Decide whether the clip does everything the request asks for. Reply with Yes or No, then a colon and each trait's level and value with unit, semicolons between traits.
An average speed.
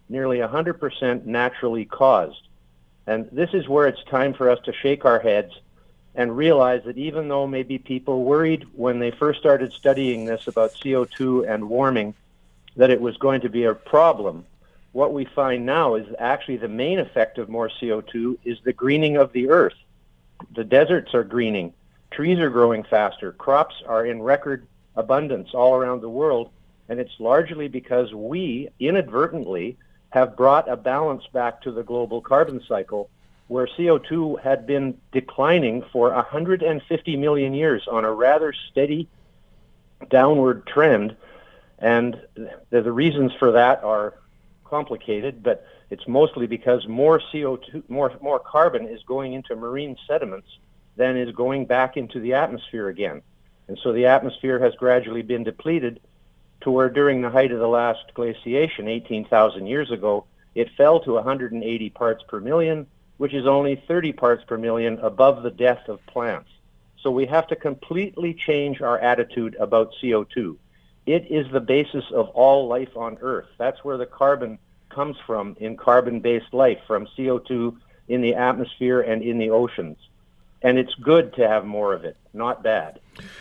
Yes: average, 160 wpm